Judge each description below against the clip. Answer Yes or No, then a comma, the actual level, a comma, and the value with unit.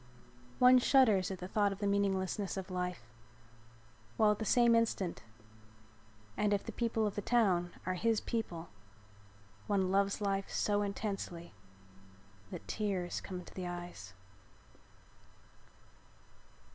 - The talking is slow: Yes, slow, 130 wpm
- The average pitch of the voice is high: Yes, high, 200 Hz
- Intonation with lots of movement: No, average, 2.8 semitones